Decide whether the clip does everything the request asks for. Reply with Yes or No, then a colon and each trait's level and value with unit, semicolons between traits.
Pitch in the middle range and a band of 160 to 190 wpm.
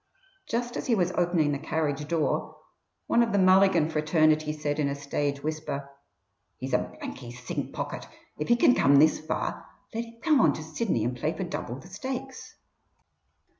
Yes: medium, 155 Hz; average, 180 wpm